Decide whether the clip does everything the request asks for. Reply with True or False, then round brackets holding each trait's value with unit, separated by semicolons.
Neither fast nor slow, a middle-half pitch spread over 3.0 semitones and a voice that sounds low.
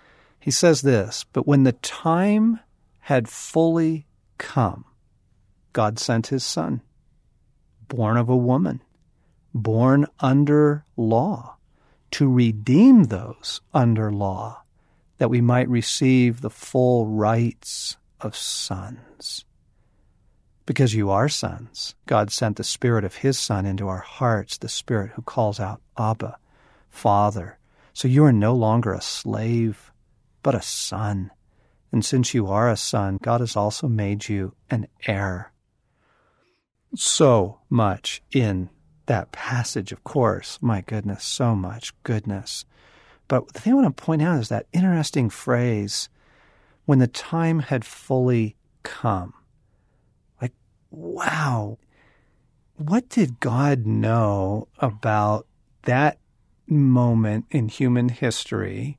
False (125 wpm; 3.9 semitones; 115 Hz)